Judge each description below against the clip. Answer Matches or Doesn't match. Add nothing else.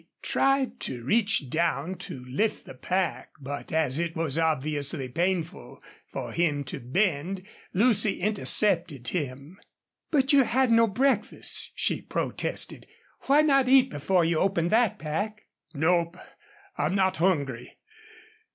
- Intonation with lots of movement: Matches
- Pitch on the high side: Doesn't match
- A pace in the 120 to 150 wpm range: Matches